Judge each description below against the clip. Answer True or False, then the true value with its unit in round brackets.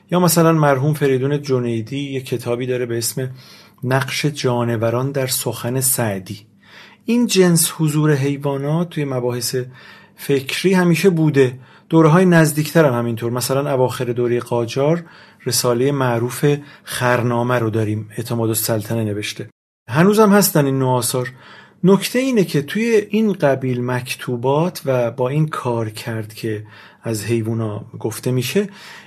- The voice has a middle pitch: False (130 Hz)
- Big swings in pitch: False (4.3 semitones)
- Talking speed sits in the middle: True (130 wpm)